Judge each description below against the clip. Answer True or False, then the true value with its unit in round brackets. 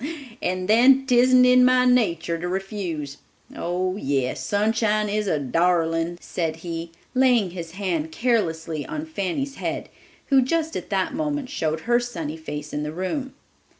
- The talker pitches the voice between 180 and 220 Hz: True (190 Hz)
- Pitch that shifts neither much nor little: False (7.2 semitones)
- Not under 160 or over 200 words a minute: False (150 wpm)